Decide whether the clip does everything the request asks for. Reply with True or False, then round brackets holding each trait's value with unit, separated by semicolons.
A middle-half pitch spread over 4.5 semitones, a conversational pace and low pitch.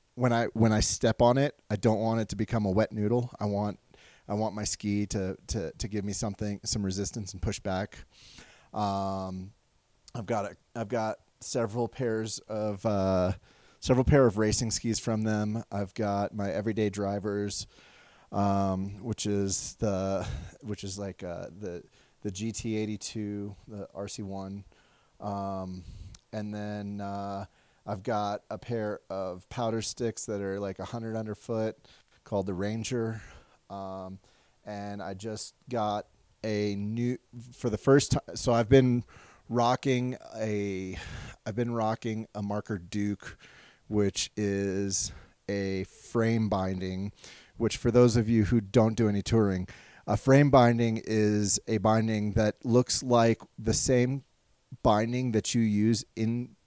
False (2.4 semitones; 155 wpm; 105 Hz)